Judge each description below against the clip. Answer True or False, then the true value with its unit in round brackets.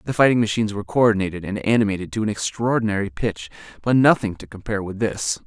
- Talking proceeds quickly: False (185 wpm)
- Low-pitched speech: True (105 Hz)